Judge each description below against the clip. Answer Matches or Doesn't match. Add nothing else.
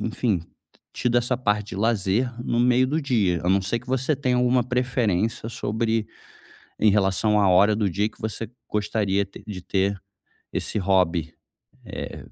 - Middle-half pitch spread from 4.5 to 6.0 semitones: Doesn't match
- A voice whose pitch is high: Doesn't match